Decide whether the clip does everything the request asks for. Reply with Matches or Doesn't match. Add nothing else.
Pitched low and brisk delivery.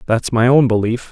Matches